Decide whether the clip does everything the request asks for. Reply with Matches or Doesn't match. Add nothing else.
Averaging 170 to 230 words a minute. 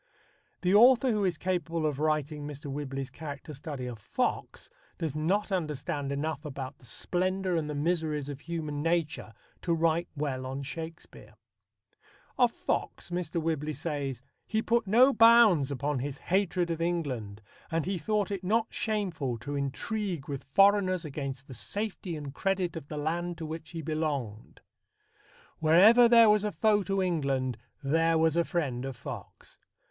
Doesn't match